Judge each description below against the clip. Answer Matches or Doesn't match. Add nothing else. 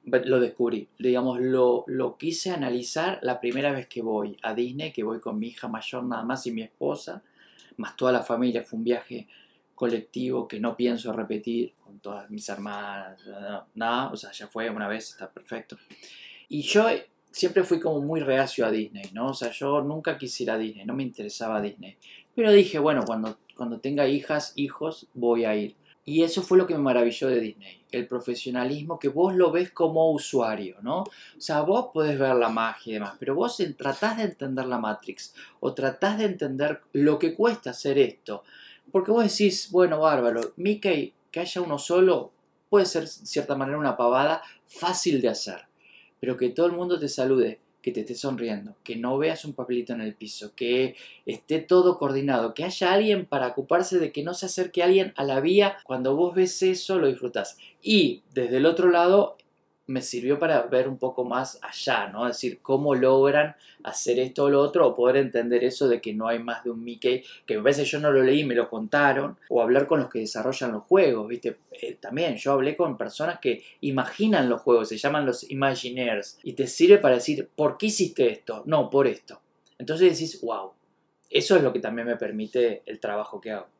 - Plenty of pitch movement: Matches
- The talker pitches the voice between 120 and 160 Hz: Matches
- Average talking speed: Doesn't match